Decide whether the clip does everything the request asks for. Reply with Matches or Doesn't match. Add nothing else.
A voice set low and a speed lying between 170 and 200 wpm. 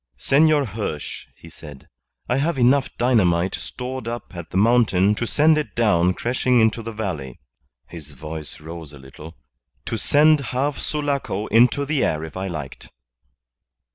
Doesn't match